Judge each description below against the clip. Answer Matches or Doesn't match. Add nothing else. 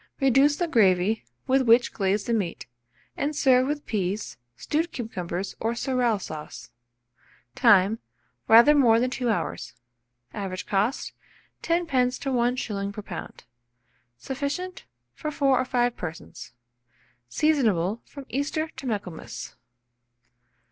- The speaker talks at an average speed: Doesn't match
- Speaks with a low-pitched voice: Doesn't match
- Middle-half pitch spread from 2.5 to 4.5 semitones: Doesn't match